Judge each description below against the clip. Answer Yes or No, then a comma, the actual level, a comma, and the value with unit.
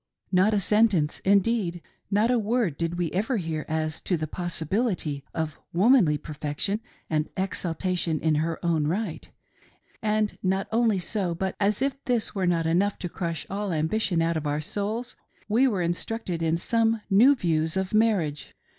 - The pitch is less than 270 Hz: Yes, medium, 185 Hz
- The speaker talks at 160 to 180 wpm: Yes, average, 165 wpm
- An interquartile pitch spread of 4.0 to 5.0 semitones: Yes, average, 4.7 semitones